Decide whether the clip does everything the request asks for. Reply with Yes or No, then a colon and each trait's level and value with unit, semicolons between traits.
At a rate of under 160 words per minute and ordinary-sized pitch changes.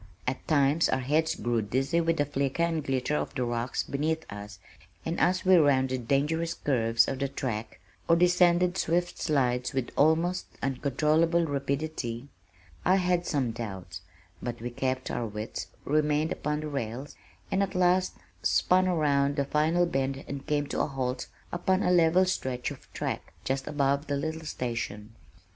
No: average, 165 wpm; average, 4.3 semitones